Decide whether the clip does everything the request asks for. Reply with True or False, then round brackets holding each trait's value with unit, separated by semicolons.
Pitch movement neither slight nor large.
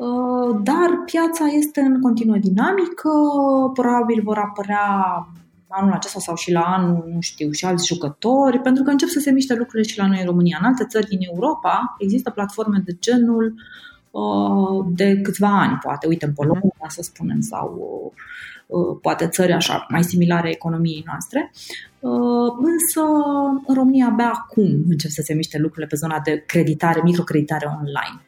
False (7.2 semitones)